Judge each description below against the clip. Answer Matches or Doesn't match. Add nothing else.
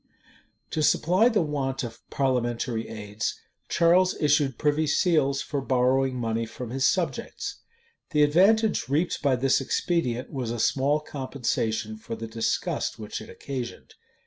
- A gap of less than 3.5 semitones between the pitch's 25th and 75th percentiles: Doesn't match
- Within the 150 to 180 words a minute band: Doesn't match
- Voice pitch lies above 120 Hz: Matches